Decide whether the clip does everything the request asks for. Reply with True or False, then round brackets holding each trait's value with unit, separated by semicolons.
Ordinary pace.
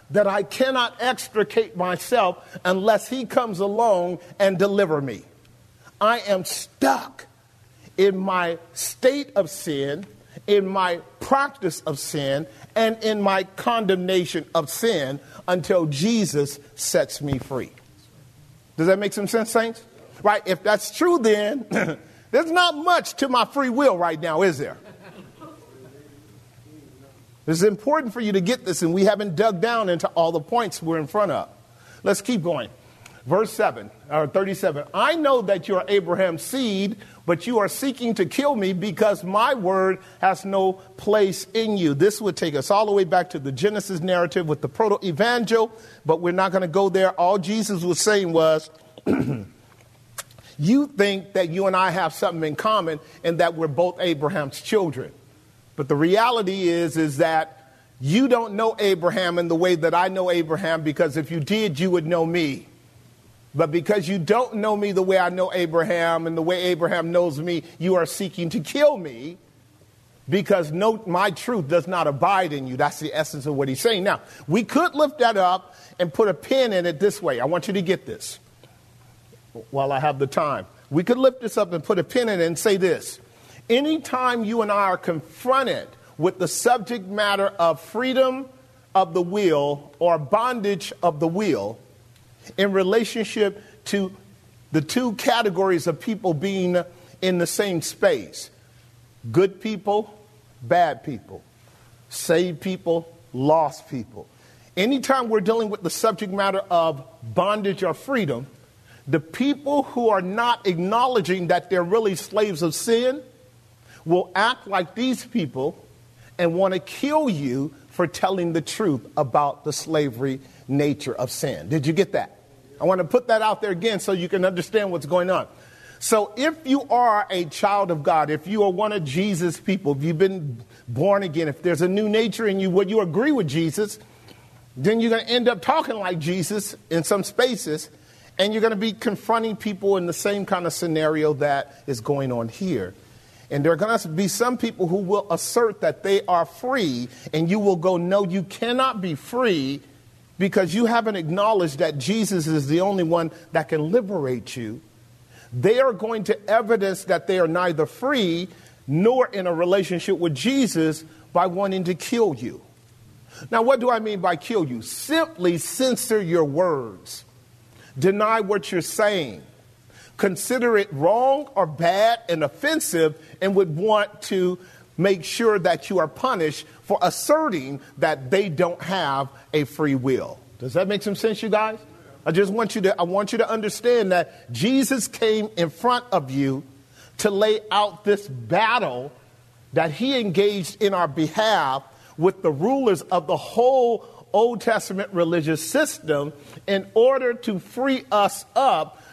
True (170 wpm)